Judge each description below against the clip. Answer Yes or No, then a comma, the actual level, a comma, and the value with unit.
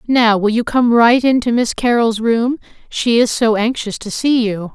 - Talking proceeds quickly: Yes, fast, 215 wpm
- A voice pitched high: Yes, high, 230 Hz